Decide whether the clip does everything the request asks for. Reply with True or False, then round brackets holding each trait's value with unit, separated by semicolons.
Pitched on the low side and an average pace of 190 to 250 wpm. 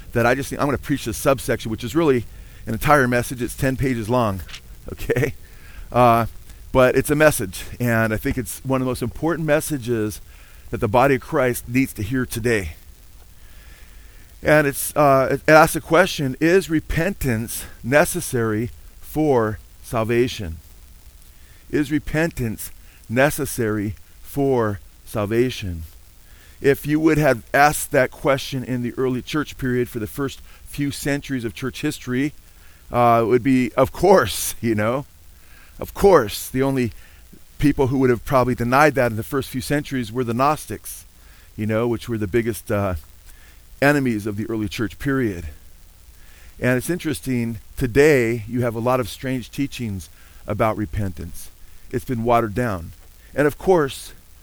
False (120 Hz; 155 wpm)